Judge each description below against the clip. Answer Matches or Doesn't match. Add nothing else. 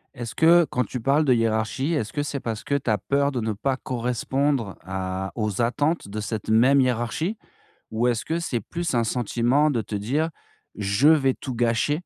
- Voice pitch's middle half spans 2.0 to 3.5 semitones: Doesn't match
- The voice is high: Doesn't match